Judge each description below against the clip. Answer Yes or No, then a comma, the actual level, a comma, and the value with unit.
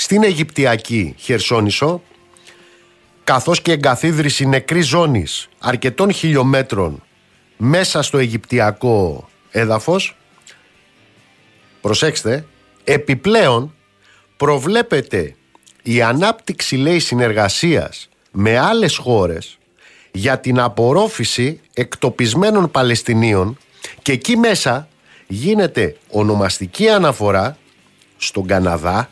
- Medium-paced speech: No, slow, 75 wpm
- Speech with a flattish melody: No, wide, 6.6 semitones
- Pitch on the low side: Yes, low, 130 Hz